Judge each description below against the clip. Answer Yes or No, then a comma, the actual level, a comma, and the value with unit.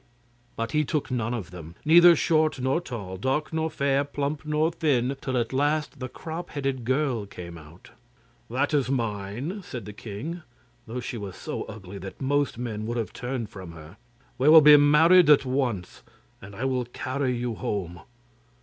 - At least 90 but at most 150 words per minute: No, average, 185 wpm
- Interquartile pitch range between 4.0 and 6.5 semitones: Yes, wide, 5.5 semitones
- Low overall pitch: Yes, low, 130 Hz